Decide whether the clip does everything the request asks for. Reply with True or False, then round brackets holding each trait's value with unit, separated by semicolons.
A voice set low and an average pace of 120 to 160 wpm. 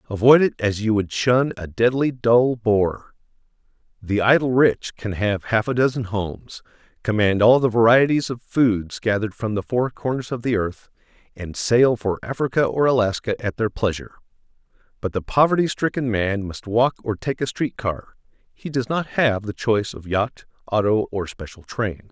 False (115 Hz; 175 wpm)